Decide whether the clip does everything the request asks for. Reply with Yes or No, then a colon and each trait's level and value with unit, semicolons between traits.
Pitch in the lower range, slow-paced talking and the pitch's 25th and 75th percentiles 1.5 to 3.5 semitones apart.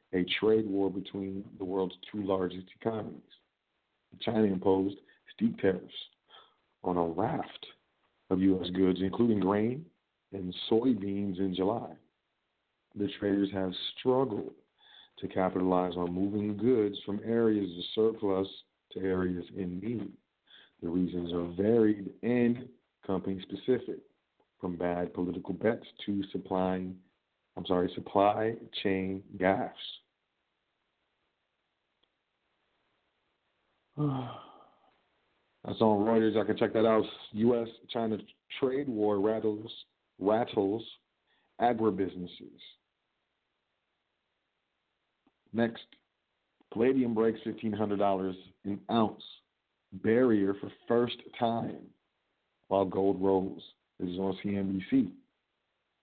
Yes: low, 100 Hz; slow, 100 wpm; average, 3.0 semitones